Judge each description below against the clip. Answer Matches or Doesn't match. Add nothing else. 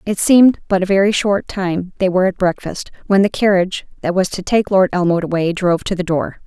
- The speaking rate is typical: Doesn't match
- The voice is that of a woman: Matches